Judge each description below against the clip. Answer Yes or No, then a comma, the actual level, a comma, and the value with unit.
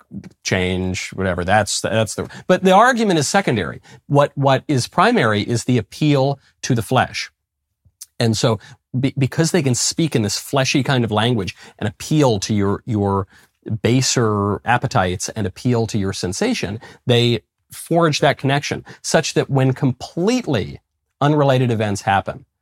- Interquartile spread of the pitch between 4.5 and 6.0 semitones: Yes, wide, 5.5 semitones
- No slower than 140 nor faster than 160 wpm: Yes, average, 150 wpm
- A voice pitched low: Yes, low, 120 Hz